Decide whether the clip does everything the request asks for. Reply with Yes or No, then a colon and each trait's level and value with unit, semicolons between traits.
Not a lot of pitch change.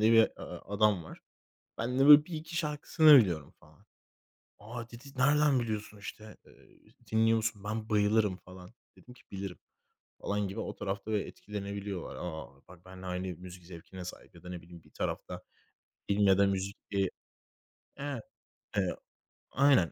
No: average, 3.9 semitones